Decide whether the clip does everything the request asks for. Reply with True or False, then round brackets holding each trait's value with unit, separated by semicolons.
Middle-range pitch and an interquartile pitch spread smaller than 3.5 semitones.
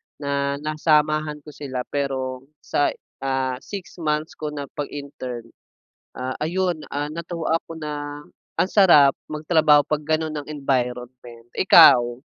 True (145 Hz; 2.6 semitones)